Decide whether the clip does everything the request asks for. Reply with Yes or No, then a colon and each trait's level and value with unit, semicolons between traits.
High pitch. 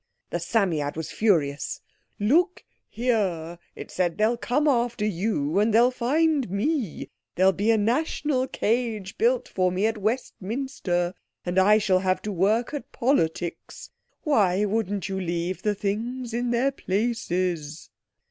Yes: high, 210 Hz